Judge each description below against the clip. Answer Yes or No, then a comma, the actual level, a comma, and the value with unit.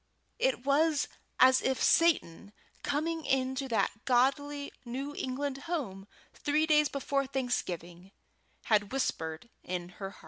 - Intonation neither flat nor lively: No, wide, 5.7 semitones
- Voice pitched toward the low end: No, very high, 265 Hz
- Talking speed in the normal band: No, slow, 125 wpm